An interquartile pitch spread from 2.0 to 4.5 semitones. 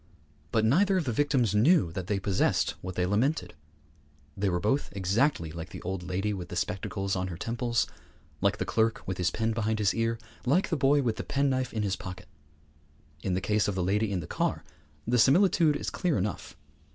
No: wide, 5.4 semitones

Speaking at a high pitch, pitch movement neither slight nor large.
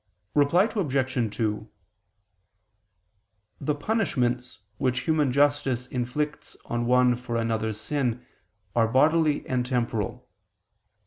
No: low, 125 Hz; average, 3.5 semitones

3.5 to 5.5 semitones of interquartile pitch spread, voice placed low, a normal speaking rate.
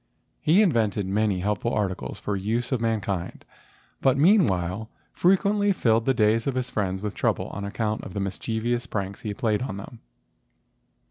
Yes: average, 3.8 semitones; low, 110 Hz; average, 175 wpm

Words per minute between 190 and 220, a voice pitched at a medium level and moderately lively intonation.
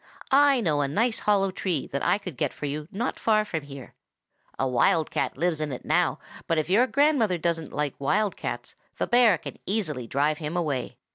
No: fast, 205 wpm; medium, 165 Hz; wide, 6.6 semitones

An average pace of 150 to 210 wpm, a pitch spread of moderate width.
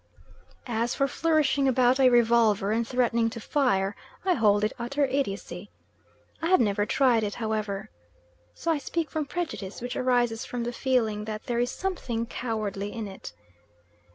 Yes: average, 160 wpm; average, 3.7 semitones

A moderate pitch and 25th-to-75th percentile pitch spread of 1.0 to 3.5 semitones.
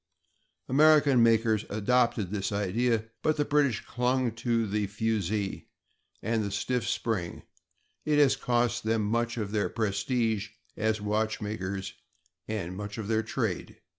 No: low, 110 Hz; average, 2.8 semitones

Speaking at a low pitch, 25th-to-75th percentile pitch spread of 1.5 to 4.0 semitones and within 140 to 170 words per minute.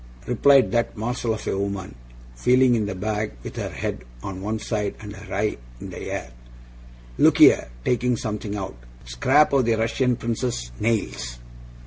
Yes: low, 110 Hz; average, 3.4 semitones; average, 165 wpm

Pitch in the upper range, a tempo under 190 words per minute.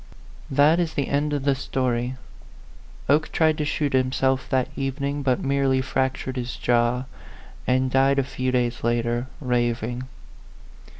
No: low, 130 Hz; average, 140 wpm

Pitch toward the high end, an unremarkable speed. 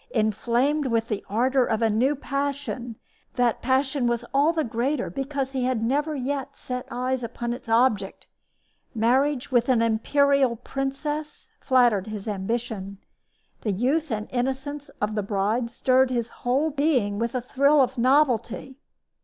Yes: very high, 250 Hz; average, 150 wpm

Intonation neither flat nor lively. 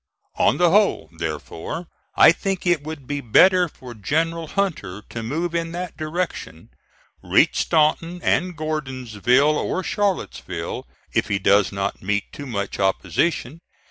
No: wide, 8.6 semitones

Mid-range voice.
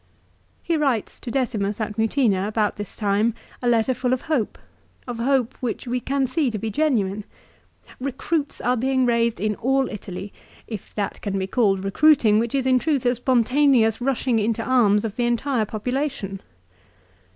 No: high, 235 Hz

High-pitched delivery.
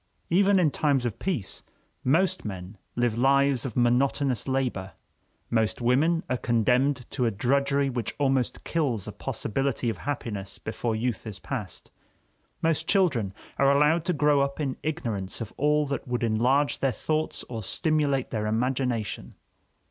No: low, 130 Hz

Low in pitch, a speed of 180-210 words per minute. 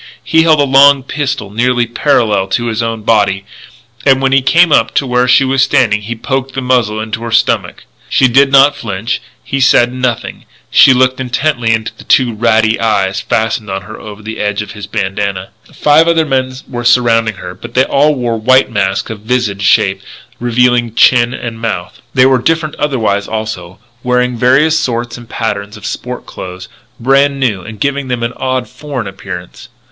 Yes: low, 120 Hz; average, 185 wpm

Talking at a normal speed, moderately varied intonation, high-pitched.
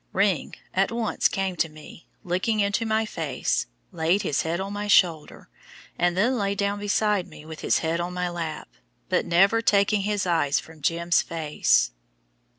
No: average, 170 wpm; average, 3.8 semitones; medium, 180 Hz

